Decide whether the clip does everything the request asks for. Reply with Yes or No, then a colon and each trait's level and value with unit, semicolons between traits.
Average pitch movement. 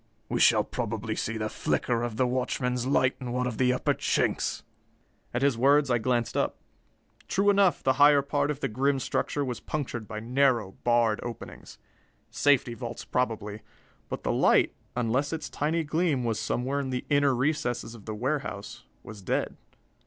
Yes: average, 3.4 semitones